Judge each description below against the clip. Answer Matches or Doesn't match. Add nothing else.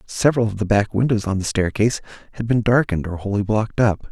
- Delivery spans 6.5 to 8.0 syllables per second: Matches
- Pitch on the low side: Matches